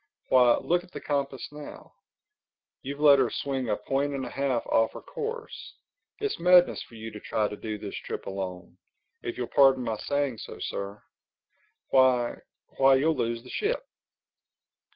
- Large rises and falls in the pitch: No, average, 4.3 semitones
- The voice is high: No, low, 130 Hz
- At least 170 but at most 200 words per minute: No, average, 160 wpm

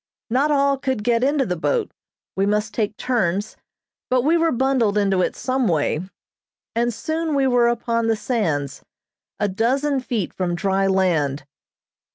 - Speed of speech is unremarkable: Yes, average, 160 wpm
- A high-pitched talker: Yes, high, 230 Hz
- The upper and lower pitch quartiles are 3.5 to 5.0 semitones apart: No, wide, 5.5 semitones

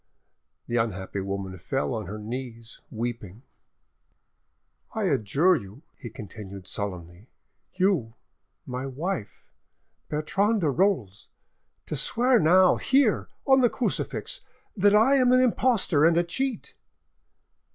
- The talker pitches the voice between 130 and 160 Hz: Yes, medium, 140 Hz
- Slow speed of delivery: Yes, slow, 120 wpm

